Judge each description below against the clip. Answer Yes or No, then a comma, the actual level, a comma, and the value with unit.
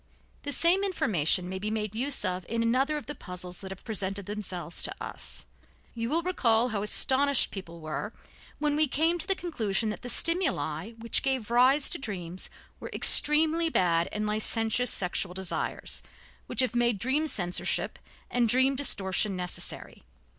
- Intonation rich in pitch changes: Yes, wide, 6.6 semitones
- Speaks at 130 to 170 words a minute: Yes, average, 165 wpm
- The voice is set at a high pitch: Yes, high, 225 Hz